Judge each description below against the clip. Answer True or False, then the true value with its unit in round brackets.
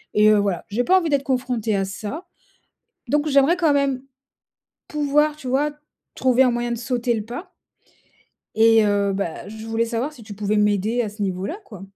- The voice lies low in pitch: False (235 Hz)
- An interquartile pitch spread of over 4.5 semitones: True (4.9 semitones)